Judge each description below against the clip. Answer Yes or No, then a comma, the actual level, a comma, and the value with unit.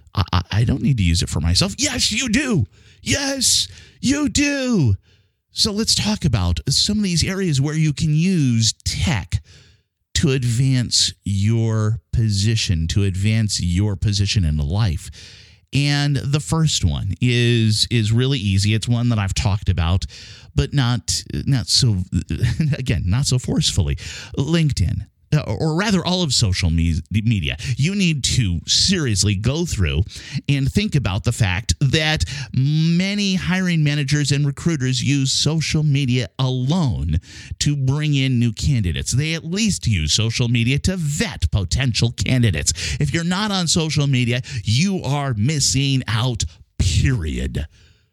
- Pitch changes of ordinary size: No, wide, 6.7 semitones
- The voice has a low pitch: Yes, low, 120 Hz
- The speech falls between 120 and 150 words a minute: Yes, average, 140 wpm